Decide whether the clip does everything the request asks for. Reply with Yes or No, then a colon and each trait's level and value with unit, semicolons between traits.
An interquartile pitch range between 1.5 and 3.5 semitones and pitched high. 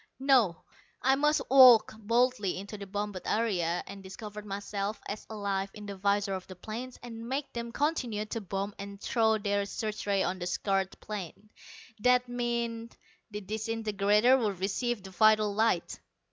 Yes: average, 2.8 semitones; high, 210 Hz